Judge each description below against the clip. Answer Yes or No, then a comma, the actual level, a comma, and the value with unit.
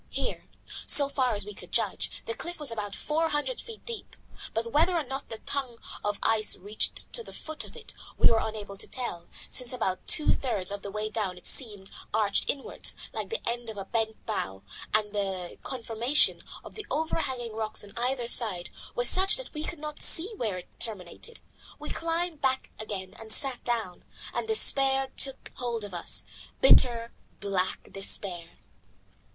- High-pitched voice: Yes, high, 235 Hz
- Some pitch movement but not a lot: No, wide, 6.0 semitones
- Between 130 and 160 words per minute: No, average, 180 wpm